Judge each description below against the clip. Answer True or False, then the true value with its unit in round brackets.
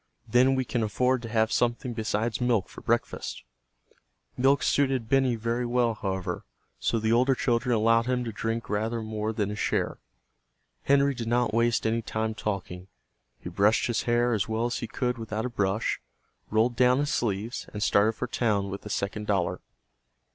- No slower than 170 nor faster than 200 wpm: True (180 wpm)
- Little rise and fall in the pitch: True (2.3 semitones)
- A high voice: False (115 Hz)